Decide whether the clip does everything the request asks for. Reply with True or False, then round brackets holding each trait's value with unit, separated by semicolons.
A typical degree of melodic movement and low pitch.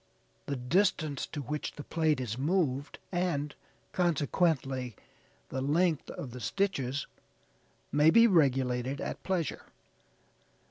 False (4.6 semitones; 145 Hz)